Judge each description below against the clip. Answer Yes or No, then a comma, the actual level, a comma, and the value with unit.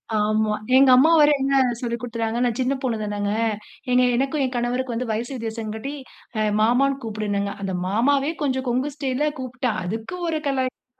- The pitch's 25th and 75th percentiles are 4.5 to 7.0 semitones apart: No, average, 3.4 semitones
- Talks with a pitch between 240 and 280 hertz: Yes, high, 245 Hz